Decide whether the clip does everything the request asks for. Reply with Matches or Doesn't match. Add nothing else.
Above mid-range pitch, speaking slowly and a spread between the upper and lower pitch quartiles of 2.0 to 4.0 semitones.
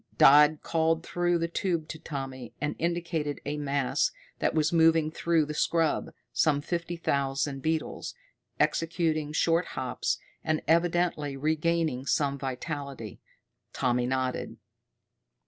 Doesn't match